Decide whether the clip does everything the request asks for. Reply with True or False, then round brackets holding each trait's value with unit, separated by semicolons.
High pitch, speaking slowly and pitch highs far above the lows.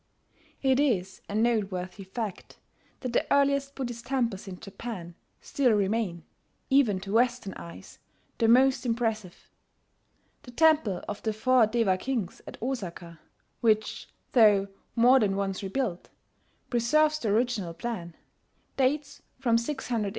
False (230 Hz; 130 wpm; 4.6 semitones)